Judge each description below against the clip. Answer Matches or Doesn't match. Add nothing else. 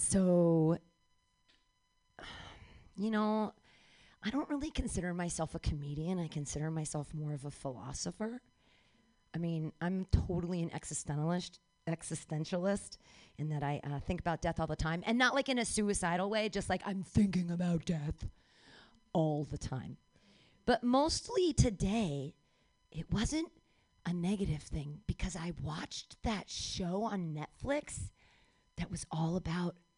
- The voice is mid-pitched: Matches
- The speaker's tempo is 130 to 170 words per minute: Matches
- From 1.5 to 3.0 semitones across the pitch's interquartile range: Doesn't match